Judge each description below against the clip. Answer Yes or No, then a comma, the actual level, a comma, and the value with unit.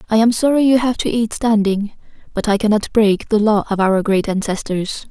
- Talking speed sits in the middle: No, fast, 210 wpm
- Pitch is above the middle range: Yes, high, 215 Hz